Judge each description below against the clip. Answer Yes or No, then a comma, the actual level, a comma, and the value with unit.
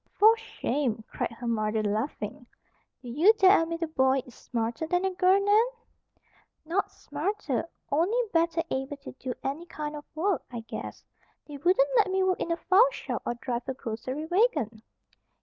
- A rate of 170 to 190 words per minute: Yes, average, 175 wpm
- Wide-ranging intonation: Yes, wide, 7.0 semitones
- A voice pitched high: Yes, very high, 310 Hz